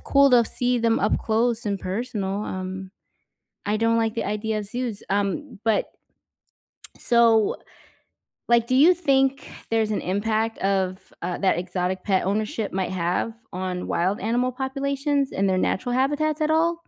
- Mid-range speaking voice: No, high, 220 Hz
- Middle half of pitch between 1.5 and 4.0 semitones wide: No, average, 4.7 semitones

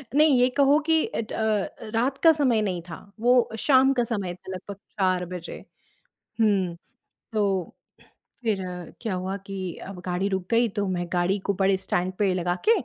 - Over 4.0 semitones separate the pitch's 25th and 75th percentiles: Yes, average, 4.5 semitones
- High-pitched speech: Yes, high, 200 Hz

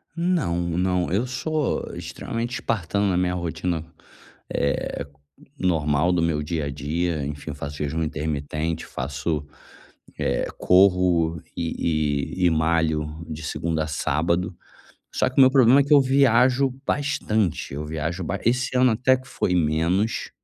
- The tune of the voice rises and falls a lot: Yes, wide, 6.8 semitones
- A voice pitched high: No, very low, 85 Hz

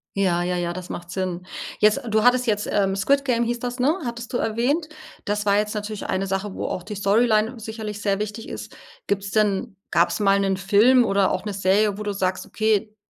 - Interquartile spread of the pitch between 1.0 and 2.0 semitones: No, narrow, 2.5 semitones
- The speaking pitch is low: No, high, 210 Hz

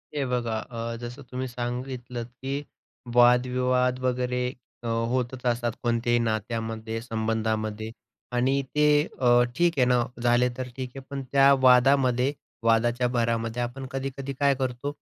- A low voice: Yes, low, 125 Hz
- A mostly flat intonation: Yes, narrow, 1.7 semitones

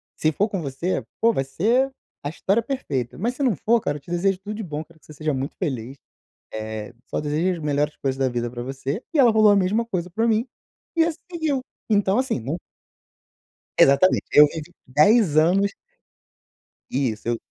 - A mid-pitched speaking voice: Yes, medium, 170 Hz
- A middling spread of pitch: No, wide, 7.7 semitones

